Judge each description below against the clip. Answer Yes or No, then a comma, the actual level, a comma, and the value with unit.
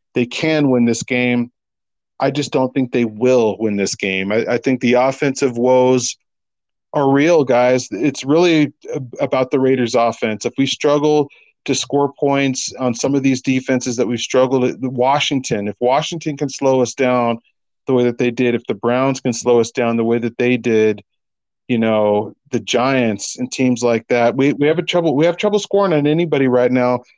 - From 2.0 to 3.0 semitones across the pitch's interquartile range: Yes, narrow, 2.5 semitones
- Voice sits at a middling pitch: No, low, 125 Hz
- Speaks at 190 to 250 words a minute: Yes, average, 195 wpm